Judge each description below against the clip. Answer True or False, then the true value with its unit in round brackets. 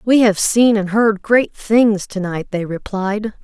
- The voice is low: False (210 Hz)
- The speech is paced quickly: False (190 wpm)